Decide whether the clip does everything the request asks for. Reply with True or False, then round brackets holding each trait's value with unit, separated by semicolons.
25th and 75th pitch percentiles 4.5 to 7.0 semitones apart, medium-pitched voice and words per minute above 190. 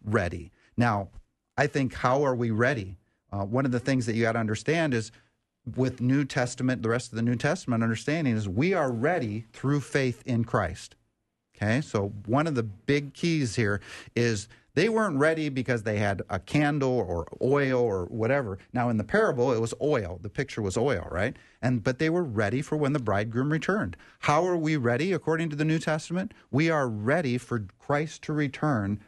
False (4.8 semitones; 125 Hz; 200 wpm)